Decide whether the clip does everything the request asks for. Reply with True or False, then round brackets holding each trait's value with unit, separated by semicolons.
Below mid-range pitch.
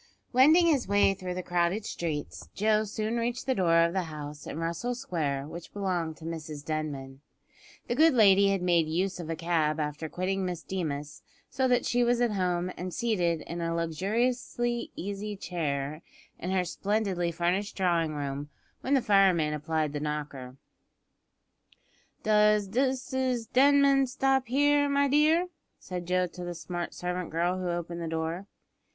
False (180 Hz)